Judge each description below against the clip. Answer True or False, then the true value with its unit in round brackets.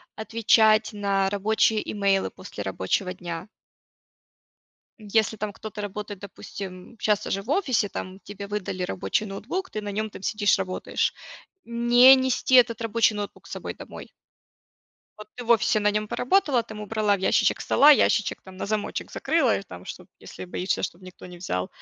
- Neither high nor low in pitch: False (210 Hz)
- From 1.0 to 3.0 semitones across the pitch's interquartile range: True (2.5 semitones)